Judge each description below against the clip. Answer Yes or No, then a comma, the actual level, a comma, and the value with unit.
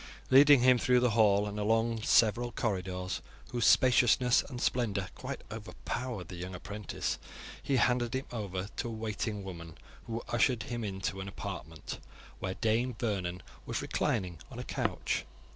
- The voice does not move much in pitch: No, average, 4.1 semitones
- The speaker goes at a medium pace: Yes, average, 155 wpm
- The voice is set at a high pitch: No, low, 110 Hz